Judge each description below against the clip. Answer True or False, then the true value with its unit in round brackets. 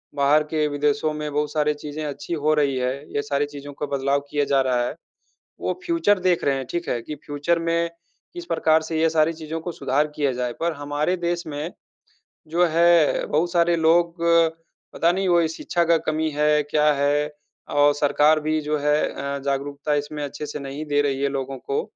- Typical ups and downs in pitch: False (2.3 semitones)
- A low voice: False (150 Hz)